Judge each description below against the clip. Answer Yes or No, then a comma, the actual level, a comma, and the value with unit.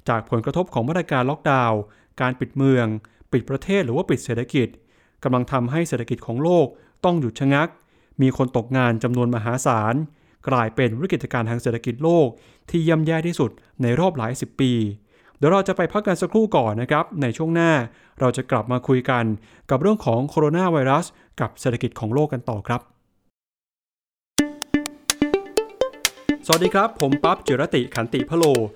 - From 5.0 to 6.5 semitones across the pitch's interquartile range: Yes, wide, 5.5 semitones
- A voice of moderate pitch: No, low, 130 Hz